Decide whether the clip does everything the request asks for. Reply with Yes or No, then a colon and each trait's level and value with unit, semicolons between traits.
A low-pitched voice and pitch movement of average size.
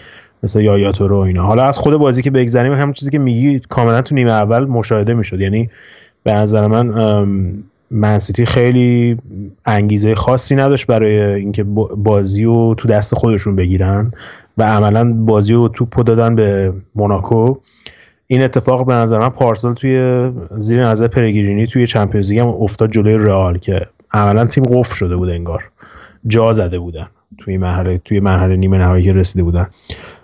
Yes: low, 110 Hz; average, 3.1 semitones